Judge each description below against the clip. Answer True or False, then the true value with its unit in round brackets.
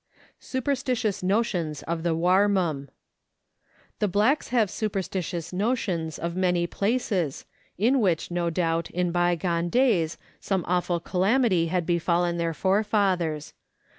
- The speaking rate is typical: False (120 wpm)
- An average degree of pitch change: True (3.5 semitones)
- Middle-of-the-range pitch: True (180 Hz)